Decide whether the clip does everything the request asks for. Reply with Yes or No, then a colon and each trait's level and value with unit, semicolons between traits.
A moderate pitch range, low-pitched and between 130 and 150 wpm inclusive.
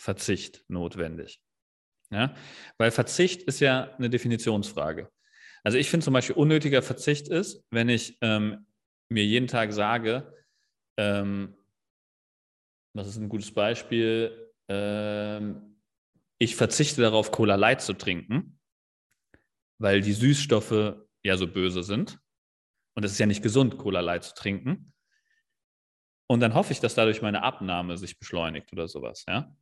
Yes: average, 4.0 semitones; low, 110 Hz; average, 140 wpm